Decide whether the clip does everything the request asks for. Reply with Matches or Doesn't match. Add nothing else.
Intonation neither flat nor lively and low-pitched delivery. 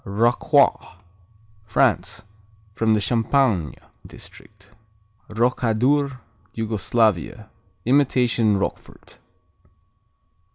Matches